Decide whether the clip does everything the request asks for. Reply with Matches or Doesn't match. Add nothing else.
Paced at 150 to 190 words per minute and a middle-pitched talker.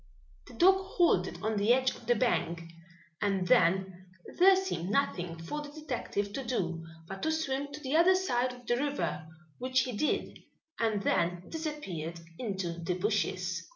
Doesn't match